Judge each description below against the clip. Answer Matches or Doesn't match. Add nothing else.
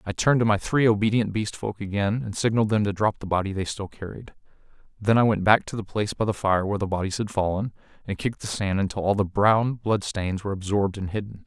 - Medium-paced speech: Doesn't match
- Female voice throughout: Doesn't match